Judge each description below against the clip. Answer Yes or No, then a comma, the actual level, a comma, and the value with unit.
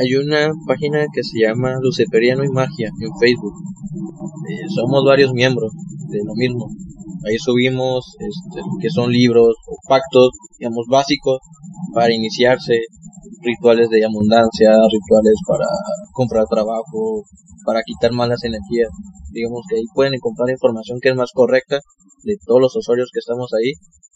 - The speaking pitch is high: No, low, 130 Hz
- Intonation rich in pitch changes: Yes, wide, 6.5 semitones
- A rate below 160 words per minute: Yes, average, 145 wpm